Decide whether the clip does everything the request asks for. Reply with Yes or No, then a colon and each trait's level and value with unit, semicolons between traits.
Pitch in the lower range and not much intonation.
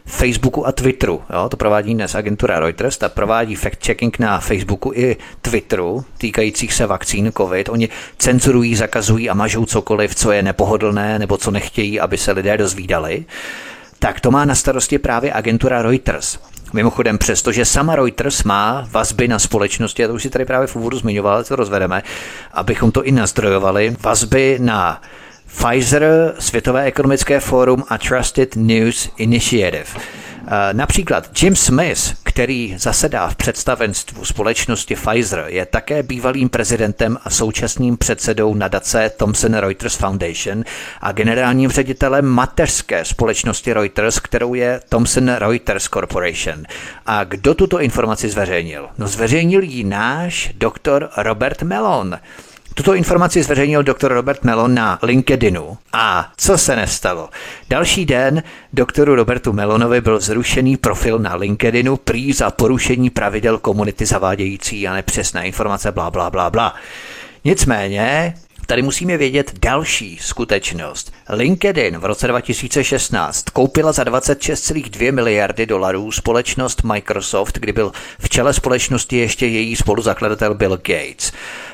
No: low, 115 Hz; average, 3.7 semitones